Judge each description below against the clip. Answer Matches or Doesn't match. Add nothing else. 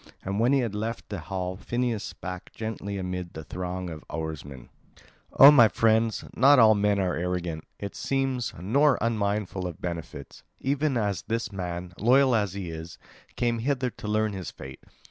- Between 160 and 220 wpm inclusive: Matches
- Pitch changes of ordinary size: Matches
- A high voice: Doesn't match